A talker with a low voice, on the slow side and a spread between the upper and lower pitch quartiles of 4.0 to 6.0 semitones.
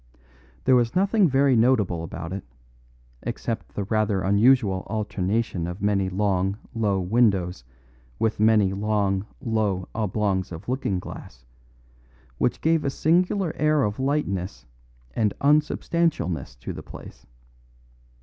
Yes: low, 105 Hz; slow, 120 wpm; wide, 5.4 semitones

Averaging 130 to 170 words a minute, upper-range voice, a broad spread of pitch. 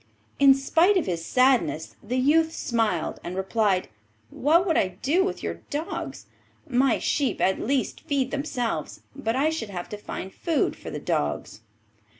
Yes: average, 160 wpm; very high, 255 Hz; wide, 7.3 semitones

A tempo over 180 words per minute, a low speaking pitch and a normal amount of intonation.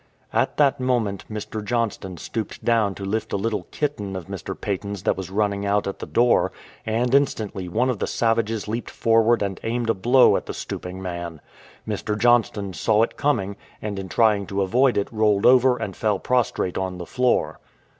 Yes: average, 190 wpm; low, 105 Hz; average, 3.4 semitones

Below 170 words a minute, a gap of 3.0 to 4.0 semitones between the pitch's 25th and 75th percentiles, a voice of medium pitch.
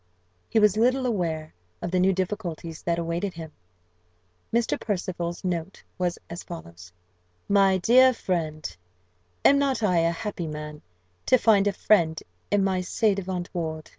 Yes: average, 150 wpm; average, 3.6 semitones; medium, 180 Hz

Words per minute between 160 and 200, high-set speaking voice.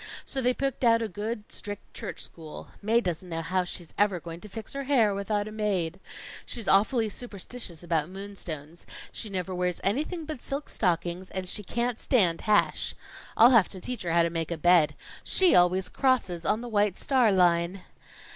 Yes: average, 190 wpm; high, 195 Hz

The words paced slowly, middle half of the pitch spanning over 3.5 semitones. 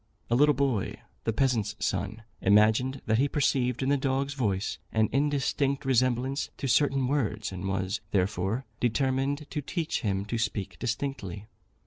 No: average, 150 wpm; average, 4.6 semitones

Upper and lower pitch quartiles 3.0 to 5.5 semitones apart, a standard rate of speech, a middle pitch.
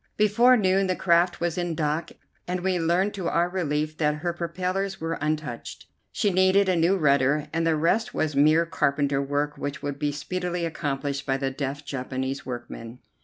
Yes: average, 4.1 semitones; average, 180 wpm; medium, 160 Hz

